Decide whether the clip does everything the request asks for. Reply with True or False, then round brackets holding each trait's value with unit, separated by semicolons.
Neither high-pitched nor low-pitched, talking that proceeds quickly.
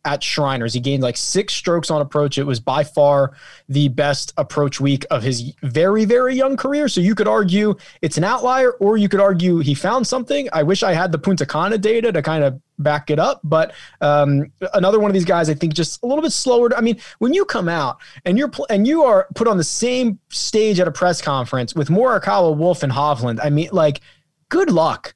True (170 Hz; 230 wpm)